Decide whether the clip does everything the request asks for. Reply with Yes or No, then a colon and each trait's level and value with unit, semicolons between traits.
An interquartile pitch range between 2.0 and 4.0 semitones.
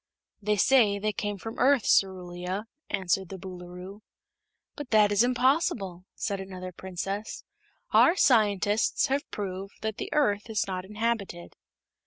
Yes: average, 2.9 semitones